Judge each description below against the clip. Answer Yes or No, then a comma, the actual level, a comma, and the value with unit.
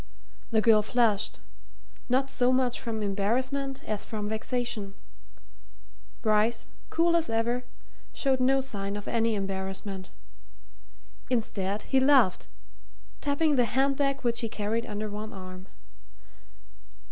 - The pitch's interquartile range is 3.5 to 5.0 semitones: Yes, average, 4.0 semitones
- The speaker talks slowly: Yes, slow, 120 wpm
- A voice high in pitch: Yes, high, 230 Hz